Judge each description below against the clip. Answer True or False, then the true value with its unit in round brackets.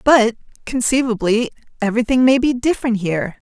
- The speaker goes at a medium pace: False (120 wpm)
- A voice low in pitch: False (235 Hz)